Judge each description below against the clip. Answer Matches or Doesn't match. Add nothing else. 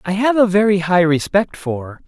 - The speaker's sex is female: Doesn't match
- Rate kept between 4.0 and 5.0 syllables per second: Matches